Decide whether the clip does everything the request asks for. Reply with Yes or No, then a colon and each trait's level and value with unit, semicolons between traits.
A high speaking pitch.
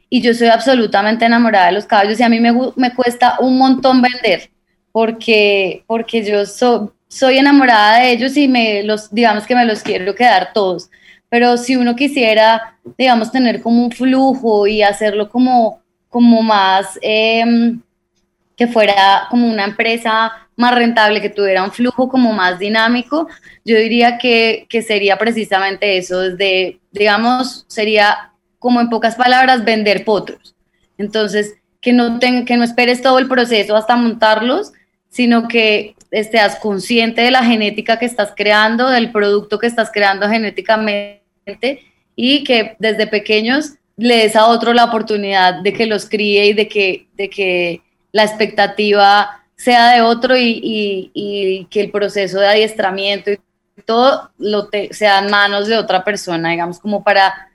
Yes: high, 220 Hz